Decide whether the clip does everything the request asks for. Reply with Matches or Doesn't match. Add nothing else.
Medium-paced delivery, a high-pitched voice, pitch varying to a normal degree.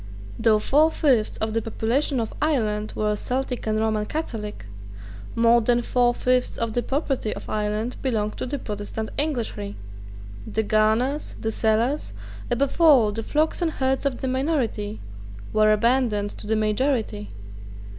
Matches